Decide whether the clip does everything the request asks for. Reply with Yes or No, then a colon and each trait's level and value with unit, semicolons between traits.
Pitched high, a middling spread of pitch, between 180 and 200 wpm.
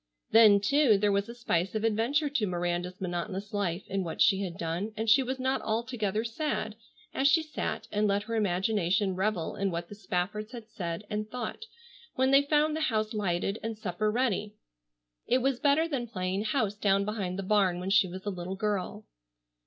Yes: high, 210 Hz; average, 3.7 semitones; average, 195 wpm